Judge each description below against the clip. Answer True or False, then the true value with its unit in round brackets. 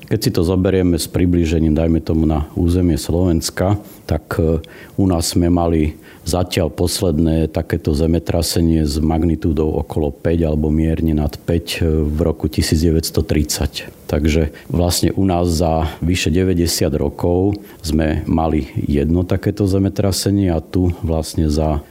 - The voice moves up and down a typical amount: False (2.3 semitones)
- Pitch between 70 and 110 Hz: True (85 Hz)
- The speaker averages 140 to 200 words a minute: False (130 wpm)